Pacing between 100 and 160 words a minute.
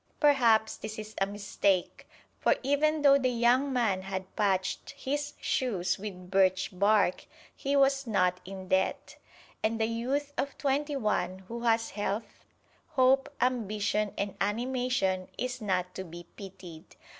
Yes: average, 145 wpm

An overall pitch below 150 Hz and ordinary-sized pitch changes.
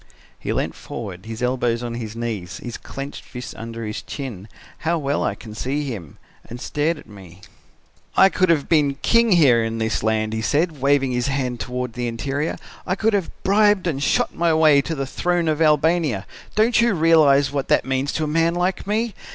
No: medium, 140 Hz; wide, 5.9 semitones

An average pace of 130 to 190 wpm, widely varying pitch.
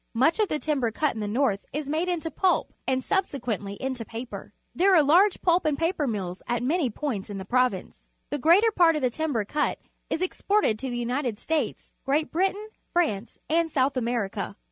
No: fast, 205 wpm; wide, 5.8 semitones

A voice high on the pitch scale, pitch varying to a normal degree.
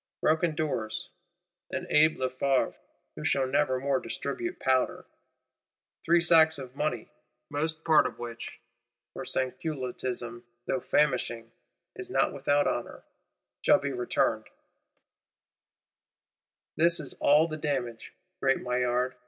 No: low, 135 Hz; average, 3.7 semitones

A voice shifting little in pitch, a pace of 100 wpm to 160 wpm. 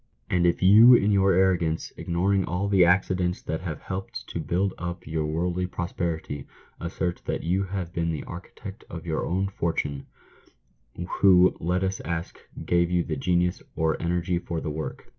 No: narrow, 2.2 semitones; average, 170 wpm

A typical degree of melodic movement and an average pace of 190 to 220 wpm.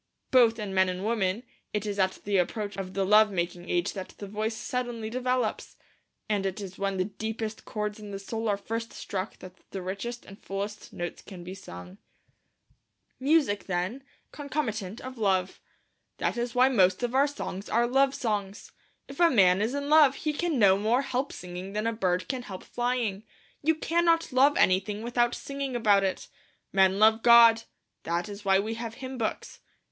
Yes: average, 4.2 semitones; average, 195 wpm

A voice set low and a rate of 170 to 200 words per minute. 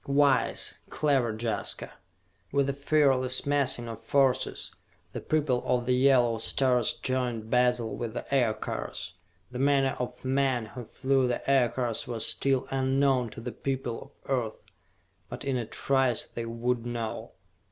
No: low, 125 Hz; average, 145 wpm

